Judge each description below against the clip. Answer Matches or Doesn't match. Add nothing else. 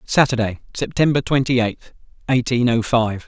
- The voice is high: Doesn't match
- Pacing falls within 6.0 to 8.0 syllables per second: Doesn't match